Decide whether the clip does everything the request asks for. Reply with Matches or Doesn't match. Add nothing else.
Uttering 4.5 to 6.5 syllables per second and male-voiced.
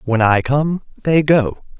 Doesn't match